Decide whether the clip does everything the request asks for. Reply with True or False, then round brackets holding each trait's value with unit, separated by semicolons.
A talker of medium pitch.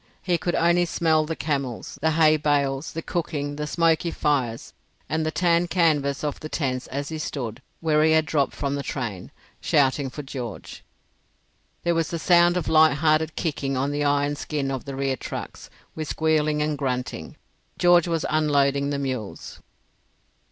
True (150 Hz)